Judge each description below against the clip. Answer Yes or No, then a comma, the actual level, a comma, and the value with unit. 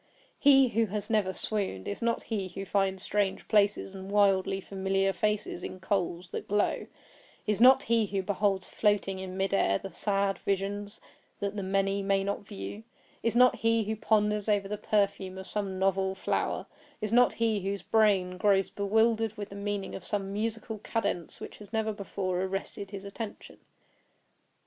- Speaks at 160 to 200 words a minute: Yes, average, 175 wpm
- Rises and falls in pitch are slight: Yes, narrow, 1.7 semitones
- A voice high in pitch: Yes, high, 200 Hz